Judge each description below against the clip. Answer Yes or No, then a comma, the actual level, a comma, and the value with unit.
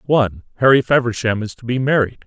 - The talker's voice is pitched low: Yes, low, 120 Hz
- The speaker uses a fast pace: No, average, 185 wpm